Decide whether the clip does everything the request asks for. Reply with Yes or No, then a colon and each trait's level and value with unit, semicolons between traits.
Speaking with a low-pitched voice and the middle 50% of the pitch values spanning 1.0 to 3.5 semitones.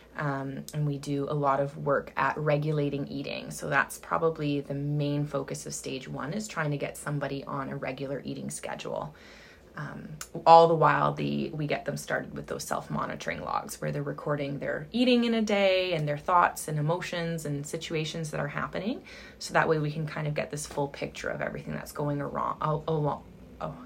No: medium, 150 Hz; narrow, 2.5 semitones